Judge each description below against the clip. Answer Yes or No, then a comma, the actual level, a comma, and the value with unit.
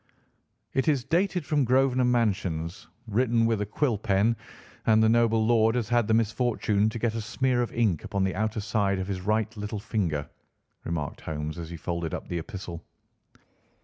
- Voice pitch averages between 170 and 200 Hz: No, low, 110 Hz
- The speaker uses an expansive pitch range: No, average, 3.7 semitones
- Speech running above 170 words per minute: Yes, average, 180 wpm